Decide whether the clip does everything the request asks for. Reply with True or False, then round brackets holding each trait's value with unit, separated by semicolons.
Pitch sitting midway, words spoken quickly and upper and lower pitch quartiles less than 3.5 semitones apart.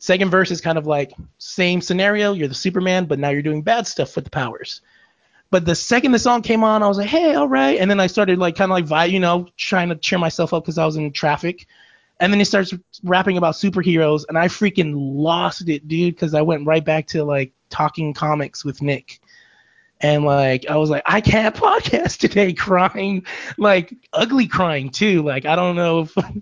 False (175 Hz; 220 wpm; 4.0 semitones)